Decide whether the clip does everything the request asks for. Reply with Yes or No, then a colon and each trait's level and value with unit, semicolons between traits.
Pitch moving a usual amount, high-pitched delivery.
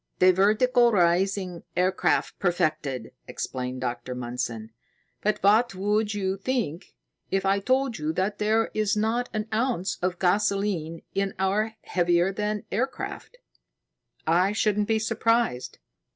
Yes: average, 3.6 semitones; high, 195 Hz